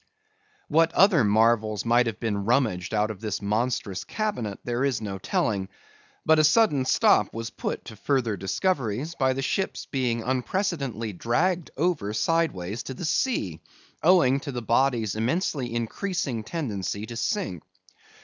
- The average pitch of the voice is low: Yes, low, 120 Hz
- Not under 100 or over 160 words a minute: Yes, average, 150 wpm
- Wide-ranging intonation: Yes, wide, 6.3 semitones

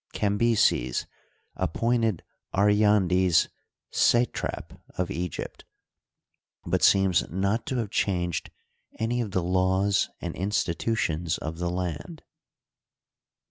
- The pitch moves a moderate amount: Yes, average, 3.4 semitones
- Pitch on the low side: Yes, very low, 95 Hz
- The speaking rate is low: Yes, slow, 100 wpm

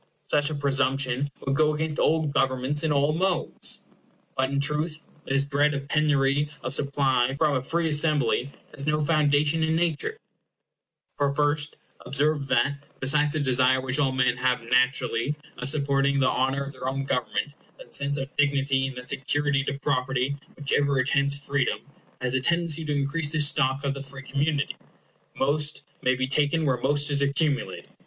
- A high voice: No, medium, 140 Hz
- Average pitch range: No, narrow, 1.9 semitones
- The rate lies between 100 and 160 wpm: No, average, 175 wpm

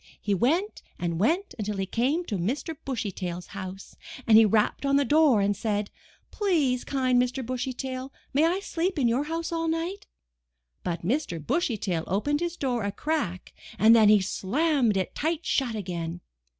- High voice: Yes, high, 245 Hz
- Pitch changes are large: Yes, wide, 7.3 semitones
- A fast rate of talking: No, average, 180 wpm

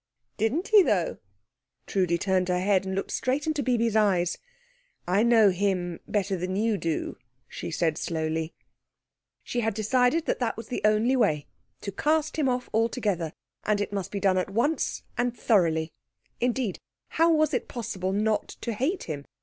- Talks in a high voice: Yes, high, 210 Hz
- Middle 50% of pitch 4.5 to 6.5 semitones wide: Yes, average, 5.1 semitones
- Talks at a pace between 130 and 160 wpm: No, average, 170 wpm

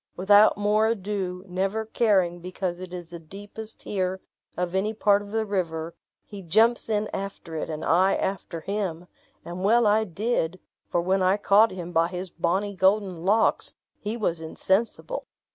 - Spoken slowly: No, average, 165 wpm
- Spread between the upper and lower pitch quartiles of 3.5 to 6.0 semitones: No, average, 2.9 semitones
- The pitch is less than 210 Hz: Yes, high, 190 Hz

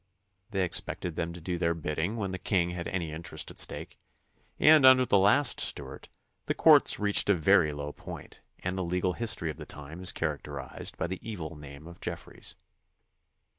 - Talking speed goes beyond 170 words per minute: Yes, average, 190 wpm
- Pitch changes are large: No, average, 3.6 semitones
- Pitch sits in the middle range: No, very low, 85 Hz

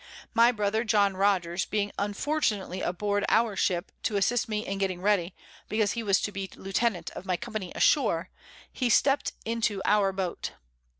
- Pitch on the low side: No, high, 205 Hz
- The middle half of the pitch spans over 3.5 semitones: No, average, 2.7 semitones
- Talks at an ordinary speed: Yes, average, 165 wpm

